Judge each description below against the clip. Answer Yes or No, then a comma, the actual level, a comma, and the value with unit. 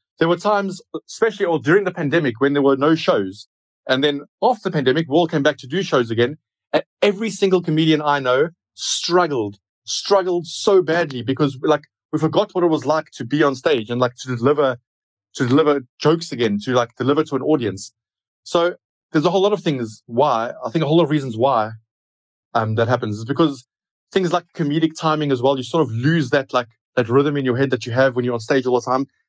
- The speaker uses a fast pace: Yes, fast, 225 wpm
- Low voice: No, medium, 145 Hz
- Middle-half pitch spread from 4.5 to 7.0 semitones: Yes, average, 4.8 semitones